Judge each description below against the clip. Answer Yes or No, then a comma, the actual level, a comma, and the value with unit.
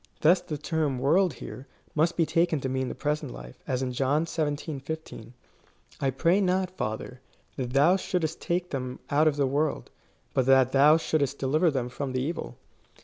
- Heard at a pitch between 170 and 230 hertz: No, medium, 145 Hz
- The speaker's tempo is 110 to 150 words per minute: No, average, 185 wpm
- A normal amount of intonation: Yes, average, 3.6 semitones